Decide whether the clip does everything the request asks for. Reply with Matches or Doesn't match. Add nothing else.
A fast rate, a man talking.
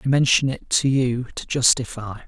Doesn't match